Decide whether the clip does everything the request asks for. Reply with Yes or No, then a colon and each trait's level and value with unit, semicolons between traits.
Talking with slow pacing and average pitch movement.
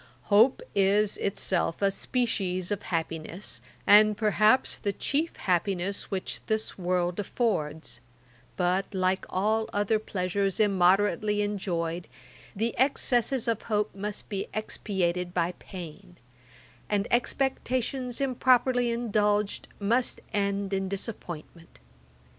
Yes: slow, 105 wpm; average, 3.1 semitones